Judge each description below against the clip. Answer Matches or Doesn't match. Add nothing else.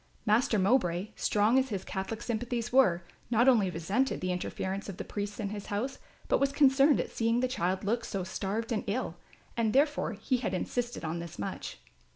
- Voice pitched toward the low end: Doesn't match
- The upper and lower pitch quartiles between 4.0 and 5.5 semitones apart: Matches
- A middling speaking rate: Matches